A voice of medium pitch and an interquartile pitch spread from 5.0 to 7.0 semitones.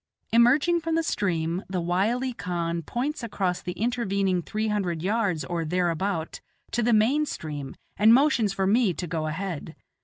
No: high, 195 Hz; wide, 5.5 semitones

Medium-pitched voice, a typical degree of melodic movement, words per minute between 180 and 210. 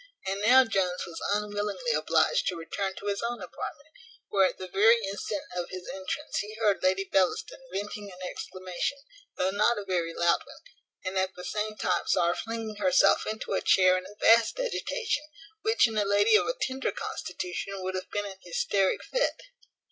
No: high, 205 Hz; average, 3.6 semitones; average, 190 wpm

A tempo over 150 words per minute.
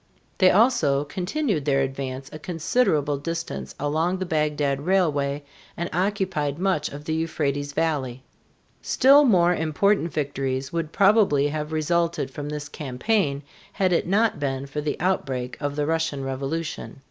No: average, 145 wpm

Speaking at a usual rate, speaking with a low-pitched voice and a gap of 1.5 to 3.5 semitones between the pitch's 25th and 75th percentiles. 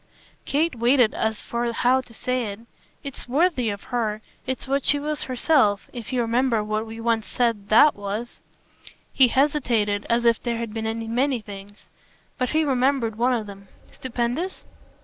No: average, 170 wpm; high, 235 Hz; average, 3.0 semitones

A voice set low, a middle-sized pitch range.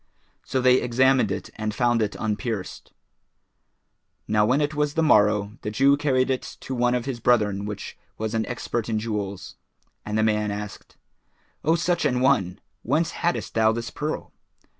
Yes: low, 115 Hz; average, 3.9 semitones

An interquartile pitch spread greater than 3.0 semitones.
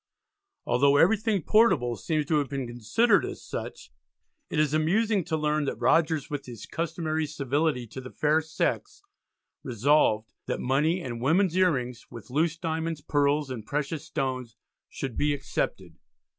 Yes: average, 3.8 semitones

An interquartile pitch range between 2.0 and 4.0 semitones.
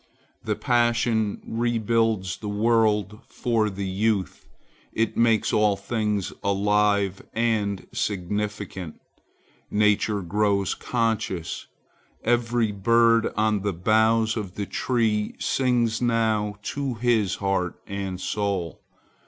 Yes: narrow, 2.4 semitones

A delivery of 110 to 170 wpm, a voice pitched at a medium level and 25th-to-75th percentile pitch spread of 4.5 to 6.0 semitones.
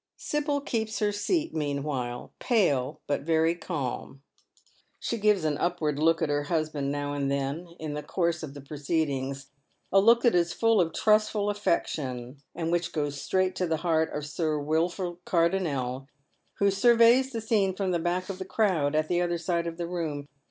No: average, 185 wpm; medium, 170 Hz; average, 4.8 semitones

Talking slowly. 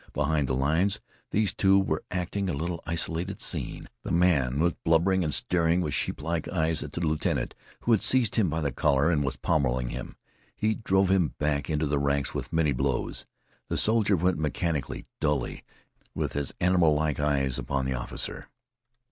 No: average, 180 wpm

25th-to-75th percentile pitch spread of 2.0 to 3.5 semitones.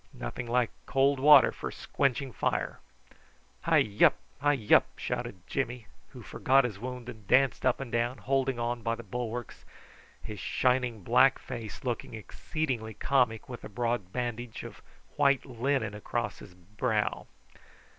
Yes: average, 3.0 semitones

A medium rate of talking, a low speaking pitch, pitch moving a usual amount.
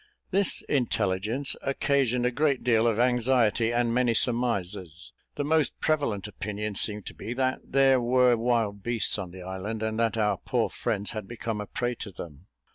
Yes: average, 175 wpm; low, 115 Hz; average, 3.3 semitones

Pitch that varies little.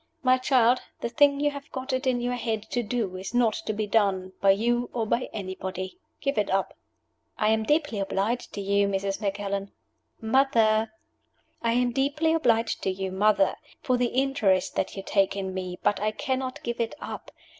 No: average, 4.2 semitones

